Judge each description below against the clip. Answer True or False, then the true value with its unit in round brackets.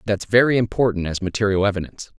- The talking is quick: False (165 wpm)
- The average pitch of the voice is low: True (105 Hz)